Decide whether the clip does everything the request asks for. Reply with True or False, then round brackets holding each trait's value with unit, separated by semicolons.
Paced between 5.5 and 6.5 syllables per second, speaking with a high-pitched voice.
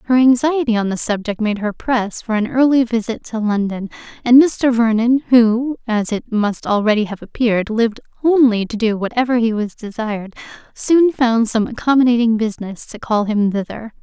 False (5.1 syllables/s; 230 Hz)